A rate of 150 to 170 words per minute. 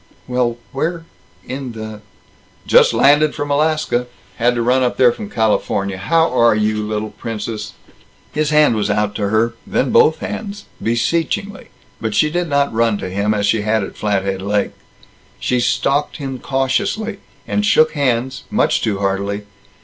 Yes: average, 165 wpm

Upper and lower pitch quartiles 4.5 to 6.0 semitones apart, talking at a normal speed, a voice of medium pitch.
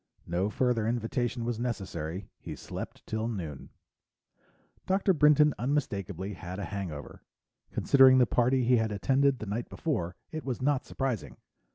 No: average, 5.2 semitones; average, 145 wpm; low, 120 Hz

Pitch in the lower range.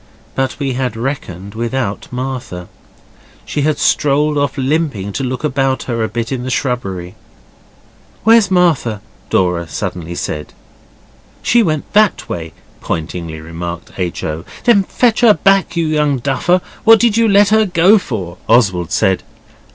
Yes: low, 130 Hz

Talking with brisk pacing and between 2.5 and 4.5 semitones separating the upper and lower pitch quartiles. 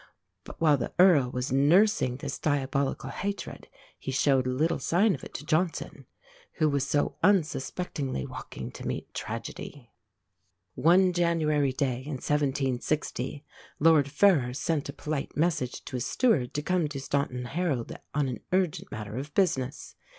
No: average, 150 wpm; average, 3.9 semitones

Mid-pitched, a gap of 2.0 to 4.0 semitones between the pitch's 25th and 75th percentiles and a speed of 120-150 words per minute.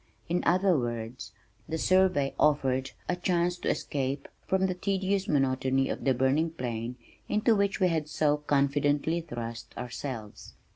No: medium, 145 Hz; average, 5.3 semitones; average, 145 wpm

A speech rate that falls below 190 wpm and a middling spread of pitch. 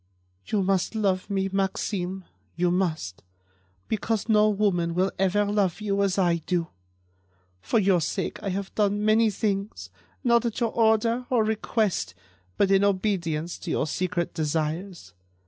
Yes: average, 145 wpm; average, 3.6 semitones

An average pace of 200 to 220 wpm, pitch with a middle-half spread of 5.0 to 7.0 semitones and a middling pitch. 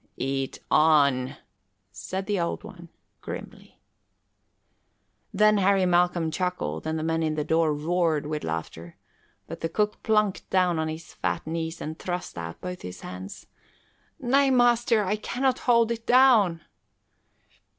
No: average, 140 wpm; average, 5.3 semitones; medium, 175 Hz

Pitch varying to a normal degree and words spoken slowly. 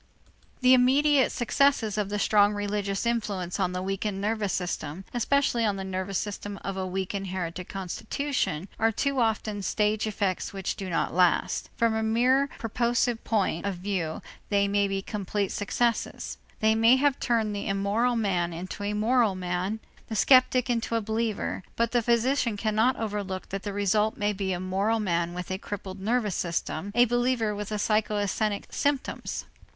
No: average, 3.1 semitones; average, 165 wpm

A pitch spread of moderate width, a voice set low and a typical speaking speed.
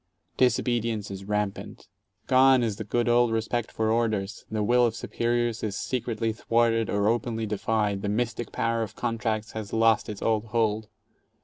No: narrow, 1.9 semitones; low, 115 Hz; average, 170 wpm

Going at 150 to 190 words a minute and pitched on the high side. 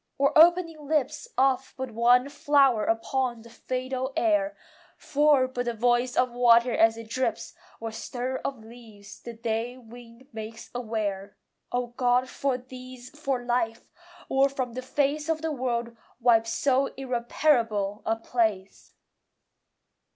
No: average, 140 wpm; high, 245 Hz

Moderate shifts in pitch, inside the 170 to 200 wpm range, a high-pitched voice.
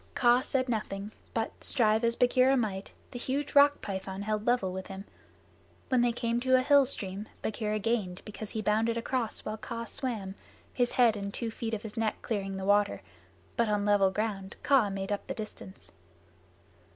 Yes: average, 3.1 semitones; average, 185 wpm; high, 220 Hz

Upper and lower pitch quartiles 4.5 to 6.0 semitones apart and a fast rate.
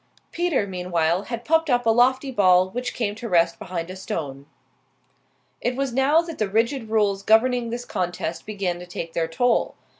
No: wide, 5.6 semitones; average, 180 wpm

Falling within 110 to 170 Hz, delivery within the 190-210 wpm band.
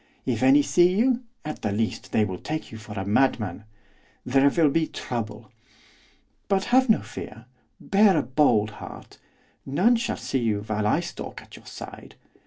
No: low, 135 Hz; average, 175 wpm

